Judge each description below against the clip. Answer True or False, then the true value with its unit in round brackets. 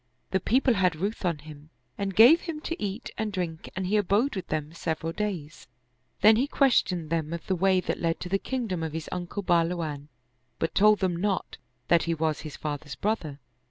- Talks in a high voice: False (180 Hz)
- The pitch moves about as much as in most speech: True (4.3 semitones)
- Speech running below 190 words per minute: False (200 wpm)